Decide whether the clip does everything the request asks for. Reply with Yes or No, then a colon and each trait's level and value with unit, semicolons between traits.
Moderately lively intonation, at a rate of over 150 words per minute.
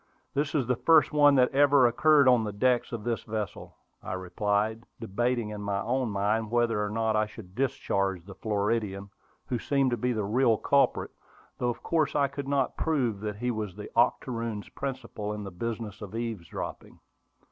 Yes: average, 3.7 semitones; average, 185 wpm